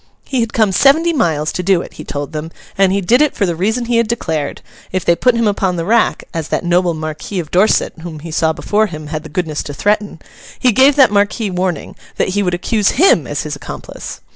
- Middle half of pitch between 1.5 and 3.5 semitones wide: No, wide, 5.5 semitones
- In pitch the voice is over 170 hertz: Yes, medium, 185 Hz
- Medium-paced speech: No, fast, 240 wpm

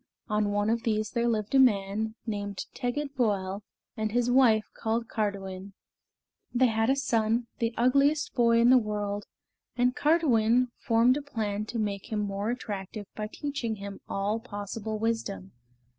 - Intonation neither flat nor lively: Yes, average, 3.0 semitones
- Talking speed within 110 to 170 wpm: Yes, average, 160 wpm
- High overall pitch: Yes, high, 220 Hz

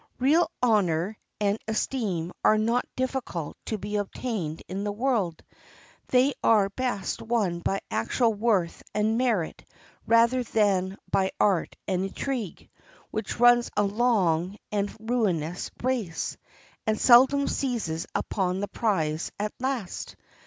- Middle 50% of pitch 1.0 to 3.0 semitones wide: No, average, 4.4 semitones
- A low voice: No, high, 210 Hz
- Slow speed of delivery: Yes, slow, 125 wpm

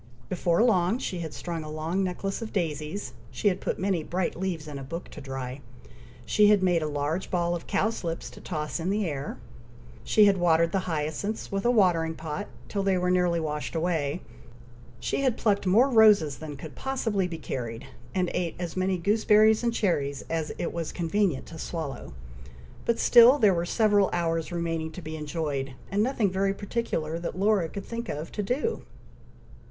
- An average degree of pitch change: Yes, average, 4.2 semitones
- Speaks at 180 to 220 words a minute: Yes, average, 190 wpm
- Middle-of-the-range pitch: Yes, medium, 175 Hz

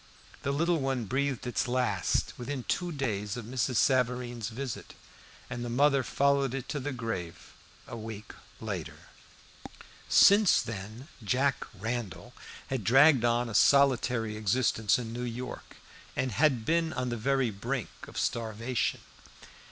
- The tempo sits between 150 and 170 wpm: No, average, 140 wpm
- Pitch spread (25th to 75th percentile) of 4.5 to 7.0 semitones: No, average, 3.2 semitones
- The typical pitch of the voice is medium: No, low, 125 Hz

